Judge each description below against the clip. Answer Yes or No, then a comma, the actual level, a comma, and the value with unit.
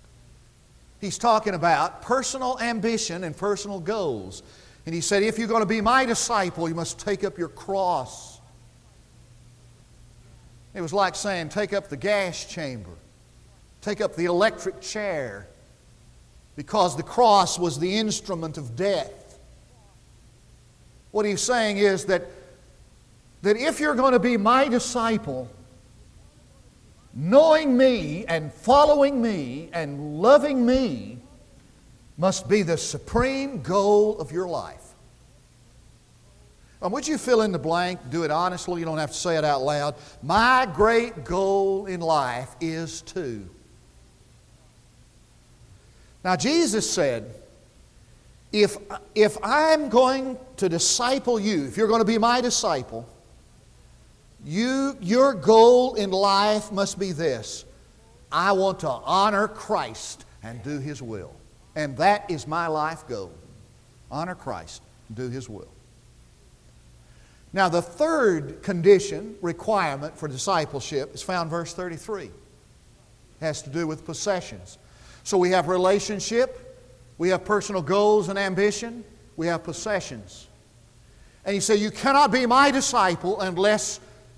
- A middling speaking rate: No, slow, 130 wpm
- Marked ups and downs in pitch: Yes, wide, 6.7 semitones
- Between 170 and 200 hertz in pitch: Yes, medium, 185 Hz